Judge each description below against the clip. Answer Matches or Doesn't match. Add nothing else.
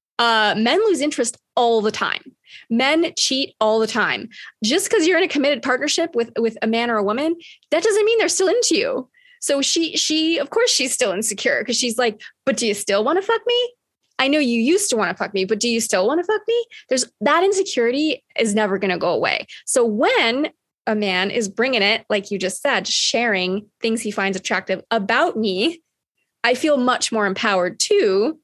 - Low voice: Doesn't match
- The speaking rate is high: Matches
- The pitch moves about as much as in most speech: Doesn't match